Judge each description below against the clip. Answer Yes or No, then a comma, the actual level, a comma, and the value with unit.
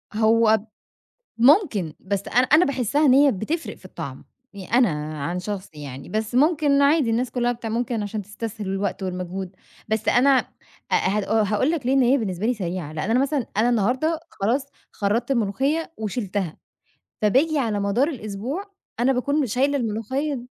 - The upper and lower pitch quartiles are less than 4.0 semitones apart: No, average, 5.2 semitones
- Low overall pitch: No, high, 230 Hz